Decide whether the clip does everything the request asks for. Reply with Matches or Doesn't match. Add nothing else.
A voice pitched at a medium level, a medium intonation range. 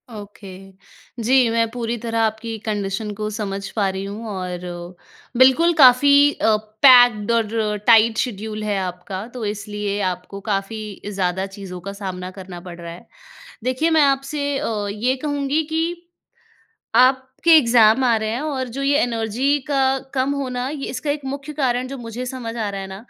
Doesn't match